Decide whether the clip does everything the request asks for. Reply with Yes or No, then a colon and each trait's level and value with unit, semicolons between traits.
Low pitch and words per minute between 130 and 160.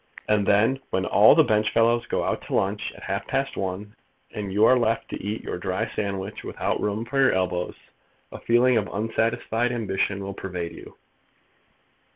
No: low, 105 Hz; average, 180 wpm